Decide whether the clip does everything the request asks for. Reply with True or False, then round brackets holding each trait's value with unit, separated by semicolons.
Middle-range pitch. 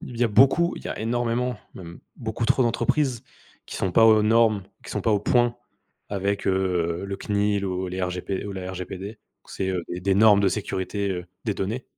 False (100 Hz)